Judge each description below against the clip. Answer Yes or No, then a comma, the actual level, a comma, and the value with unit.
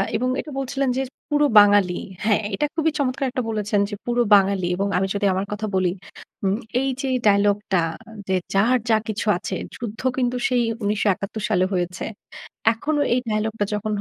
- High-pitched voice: Yes, high, 210 Hz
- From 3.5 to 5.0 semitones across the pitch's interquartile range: Yes, average, 4.0 semitones